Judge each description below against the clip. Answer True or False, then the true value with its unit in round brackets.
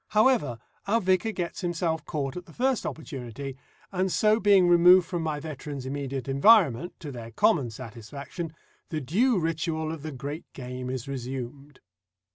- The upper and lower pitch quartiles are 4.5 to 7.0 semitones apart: True (5.1 semitones)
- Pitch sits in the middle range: True (155 Hz)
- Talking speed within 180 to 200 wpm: False (155 wpm)